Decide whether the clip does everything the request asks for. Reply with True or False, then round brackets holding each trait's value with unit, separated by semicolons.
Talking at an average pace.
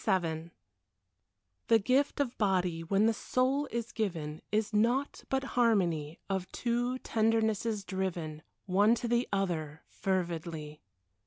False (125 wpm)